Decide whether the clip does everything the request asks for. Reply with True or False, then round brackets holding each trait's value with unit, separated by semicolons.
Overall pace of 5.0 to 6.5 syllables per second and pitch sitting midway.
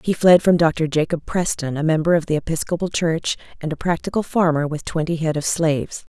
True (5.6 syllables/s; 160 Hz)